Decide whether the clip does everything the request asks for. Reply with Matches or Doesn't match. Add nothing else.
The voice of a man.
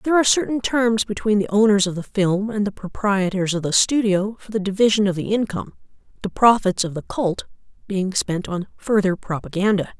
Doesn't match